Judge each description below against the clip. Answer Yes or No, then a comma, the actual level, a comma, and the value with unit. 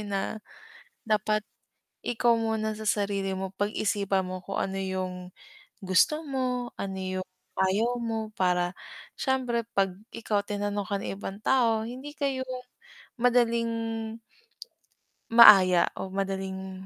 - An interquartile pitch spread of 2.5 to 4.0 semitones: Yes, average, 3.4 semitones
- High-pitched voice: Yes, high, 205 Hz